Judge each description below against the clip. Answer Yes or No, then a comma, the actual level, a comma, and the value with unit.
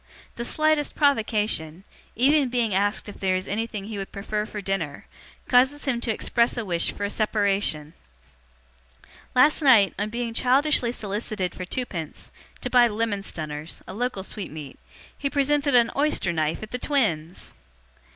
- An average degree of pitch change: Yes, average, 4.6 semitones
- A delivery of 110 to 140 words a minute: No, average, 155 wpm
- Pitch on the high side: Yes, high, 215 Hz